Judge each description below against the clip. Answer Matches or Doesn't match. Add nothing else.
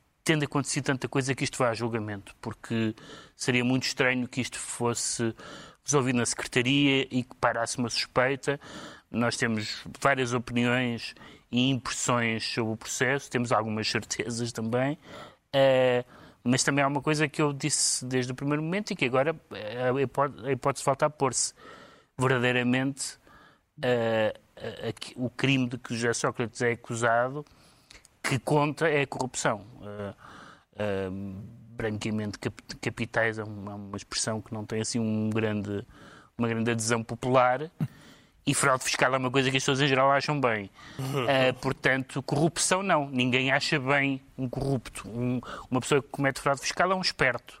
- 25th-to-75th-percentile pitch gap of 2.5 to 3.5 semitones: Matches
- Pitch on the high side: Doesn't match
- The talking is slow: Doesn't match